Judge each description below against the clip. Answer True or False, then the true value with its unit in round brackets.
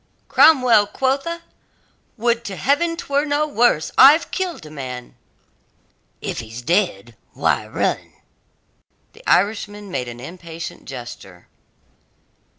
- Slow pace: True (110 wpm)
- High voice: True (205 Hz)